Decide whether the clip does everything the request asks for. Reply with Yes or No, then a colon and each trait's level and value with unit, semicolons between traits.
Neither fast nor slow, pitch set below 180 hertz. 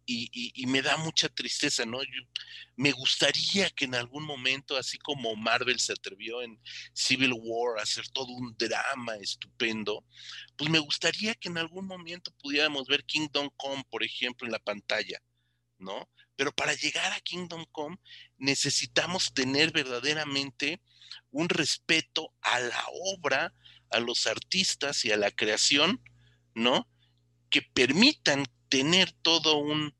Yes: average, 145 wpm; medium, 140 Hz